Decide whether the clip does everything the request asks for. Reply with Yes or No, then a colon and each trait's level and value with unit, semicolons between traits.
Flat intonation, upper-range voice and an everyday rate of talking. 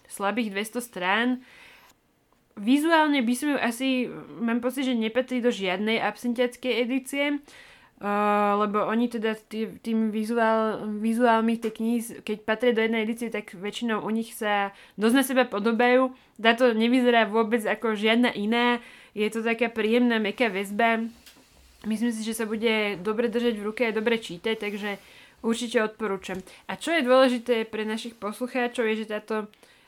Yes: narrow, 2.1 semitones; high, 230 Hz; average, 155 wpm